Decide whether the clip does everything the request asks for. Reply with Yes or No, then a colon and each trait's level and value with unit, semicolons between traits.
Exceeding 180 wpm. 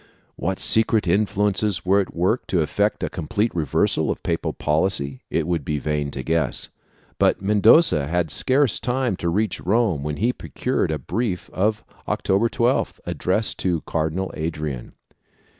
No: average, 155 wpm